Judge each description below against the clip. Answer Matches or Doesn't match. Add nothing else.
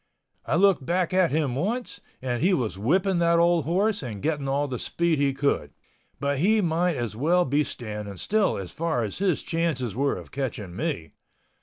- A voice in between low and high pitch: Matches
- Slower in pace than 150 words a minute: Doesn't match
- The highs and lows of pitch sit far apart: Matches